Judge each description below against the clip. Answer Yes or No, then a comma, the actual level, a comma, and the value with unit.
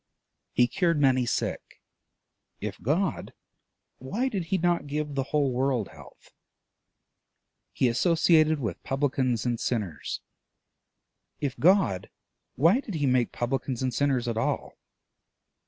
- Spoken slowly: Yes, slow, 120 wpm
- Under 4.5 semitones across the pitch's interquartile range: No, average, 4.8 semitones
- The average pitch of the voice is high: No, low, 135 Hz